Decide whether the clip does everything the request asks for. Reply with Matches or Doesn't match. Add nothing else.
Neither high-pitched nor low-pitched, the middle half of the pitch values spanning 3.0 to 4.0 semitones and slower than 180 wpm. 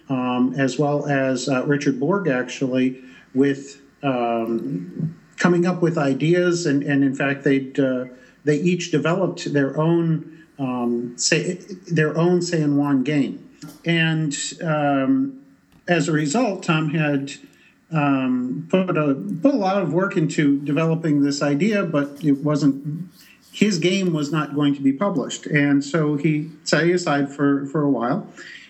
Matches